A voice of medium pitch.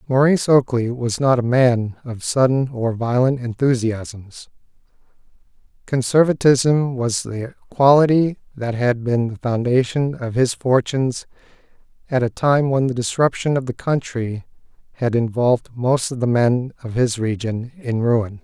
No: low, 125 Hz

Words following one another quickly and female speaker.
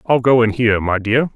No: fast, 265 wpm; male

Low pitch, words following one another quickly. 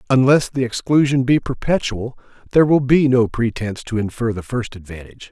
No: low, 125 Hz; average, 170 wpm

